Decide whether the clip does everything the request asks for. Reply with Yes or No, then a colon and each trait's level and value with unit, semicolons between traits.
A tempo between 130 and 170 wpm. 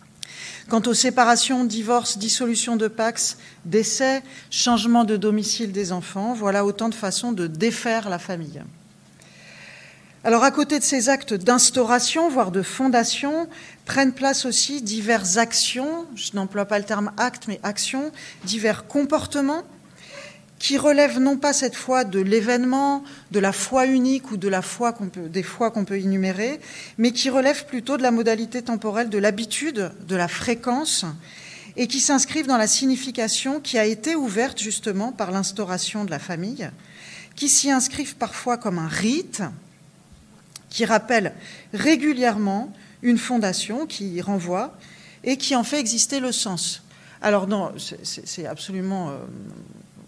Yes: average, 150 wpm